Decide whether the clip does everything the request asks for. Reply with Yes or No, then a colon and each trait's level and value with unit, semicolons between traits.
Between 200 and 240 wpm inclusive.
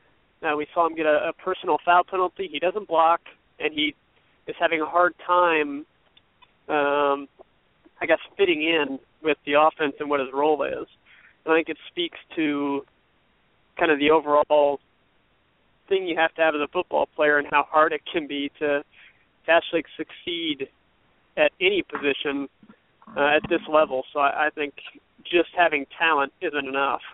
No: average, 170 wpm